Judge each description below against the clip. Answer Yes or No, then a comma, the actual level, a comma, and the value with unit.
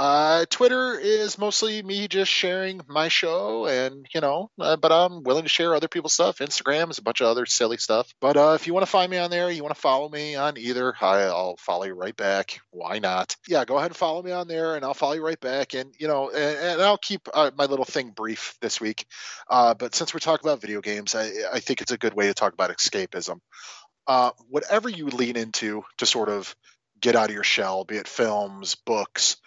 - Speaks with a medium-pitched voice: Yes, medium, 150 Hz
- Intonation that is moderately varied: No, wide, 6.9 semitones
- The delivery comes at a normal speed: No, fast, 240 wpm